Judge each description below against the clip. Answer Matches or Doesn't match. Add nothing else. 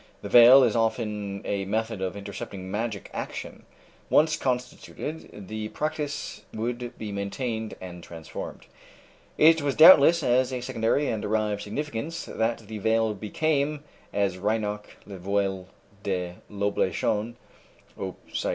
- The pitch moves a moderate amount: Matches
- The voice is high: Doesn't match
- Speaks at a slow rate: Matches